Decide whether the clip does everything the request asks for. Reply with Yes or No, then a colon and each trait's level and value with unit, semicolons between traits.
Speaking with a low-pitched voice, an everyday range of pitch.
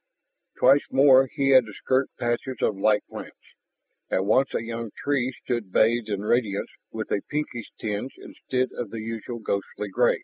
Yes: low, 115 Hz; average, 3.4 semitones